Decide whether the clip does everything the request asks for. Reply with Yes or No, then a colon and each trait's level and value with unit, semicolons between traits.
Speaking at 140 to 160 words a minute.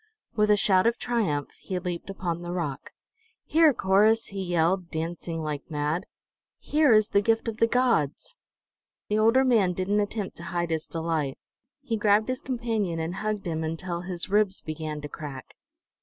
No: average, 170 wpm